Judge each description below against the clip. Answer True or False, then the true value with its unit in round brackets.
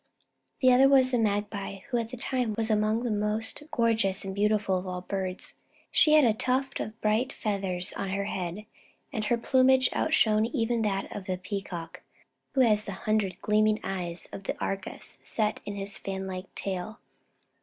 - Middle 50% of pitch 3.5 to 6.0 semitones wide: False (3.0 semitones)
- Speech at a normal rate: True (180 wpm)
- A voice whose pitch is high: True (210 Hz)